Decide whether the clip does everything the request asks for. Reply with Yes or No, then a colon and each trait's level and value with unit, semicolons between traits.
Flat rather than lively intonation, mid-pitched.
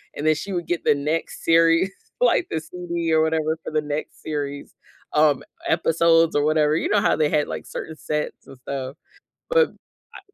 Yes: narrow, 1.8 semitones; medium, 155 Hz